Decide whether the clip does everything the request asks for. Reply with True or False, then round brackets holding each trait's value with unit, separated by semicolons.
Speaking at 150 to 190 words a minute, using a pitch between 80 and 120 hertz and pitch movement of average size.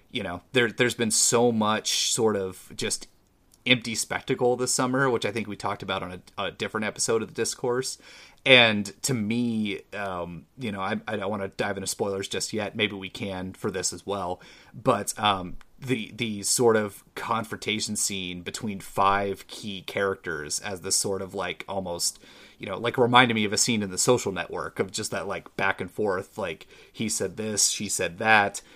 False (200 wpm; 105 Hz; 3.5 semitones)